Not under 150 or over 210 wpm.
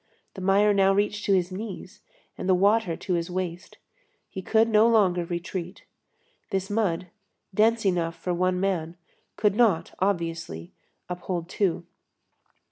No: average, 140 wpm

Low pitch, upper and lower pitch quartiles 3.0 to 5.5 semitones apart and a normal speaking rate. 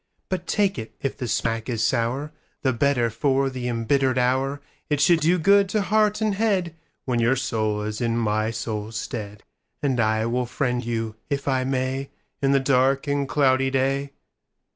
Yes: low, 130 Hz; average, 3.4 semitones; average, 160 wpm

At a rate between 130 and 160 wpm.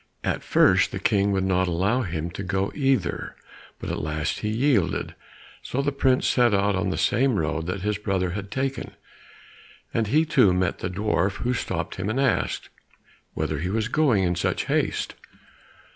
No: average, 180 wpm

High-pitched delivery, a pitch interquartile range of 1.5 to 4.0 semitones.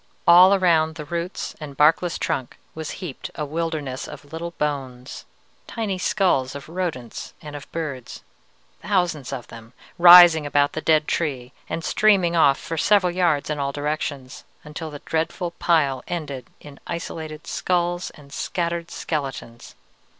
No: medium, 155 Hz; average, 3.3 semitones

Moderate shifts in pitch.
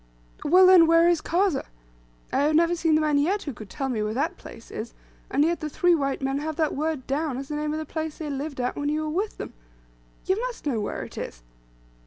Yes: average, 3.2 semitones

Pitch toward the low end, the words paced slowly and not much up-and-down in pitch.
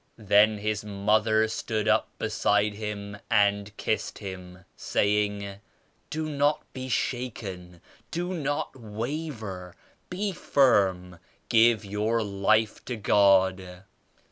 No: low, 105 Hz; slow, 105 wpm; average, 3.1 semitones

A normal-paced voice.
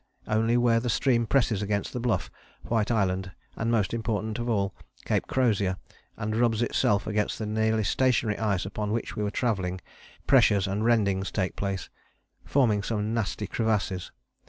Yes: average, 160 wpm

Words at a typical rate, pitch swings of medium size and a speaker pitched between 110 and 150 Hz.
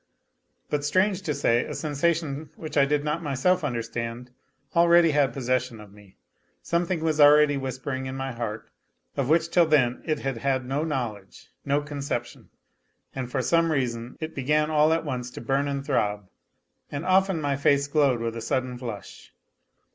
Yes: average, 175 wpm; average, 3.8 semitones; medium, 140 Hz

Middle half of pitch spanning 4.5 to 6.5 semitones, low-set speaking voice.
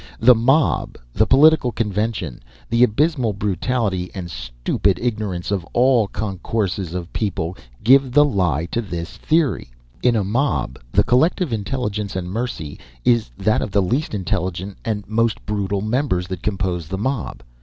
Yes: average, 4.9 semitones; low, 105 Hz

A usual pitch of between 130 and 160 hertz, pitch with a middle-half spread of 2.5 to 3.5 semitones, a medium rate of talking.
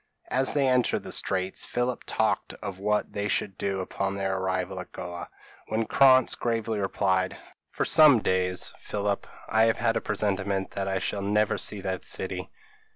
No: low, 100 Hz; average, 2.9 semitones; average, 170 wpm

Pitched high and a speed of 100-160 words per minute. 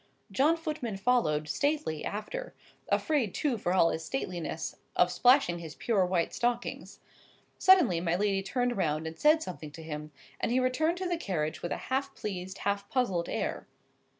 No: high, 200 Hz; average, 170 wpm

